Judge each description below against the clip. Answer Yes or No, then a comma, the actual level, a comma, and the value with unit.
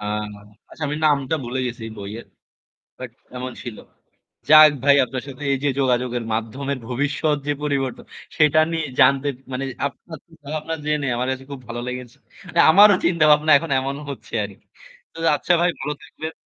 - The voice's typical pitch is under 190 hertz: Yes, medium, 140 Hz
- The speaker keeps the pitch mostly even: No, average, 3.3 semitones